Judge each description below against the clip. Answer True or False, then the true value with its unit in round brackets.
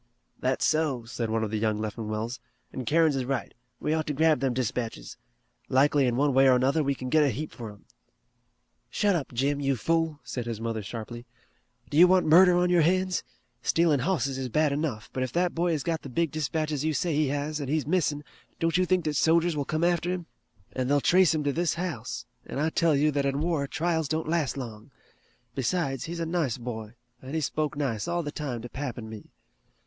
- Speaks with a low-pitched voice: False (145 Hz)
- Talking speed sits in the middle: False (225 wpm)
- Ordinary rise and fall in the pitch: True (4.3 semitones)